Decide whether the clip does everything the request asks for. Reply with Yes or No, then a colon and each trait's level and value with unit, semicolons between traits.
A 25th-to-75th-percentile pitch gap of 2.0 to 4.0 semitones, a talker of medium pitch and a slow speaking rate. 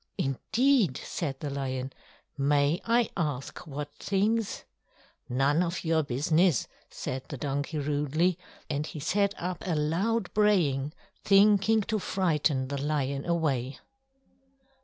No: average, 5.2 semitones; medium, 155 Hz; slow, 120 wpm